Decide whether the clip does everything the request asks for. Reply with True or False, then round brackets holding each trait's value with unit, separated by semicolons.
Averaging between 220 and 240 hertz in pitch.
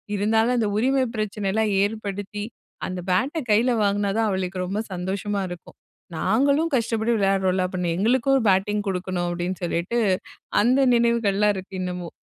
False (205 Hz)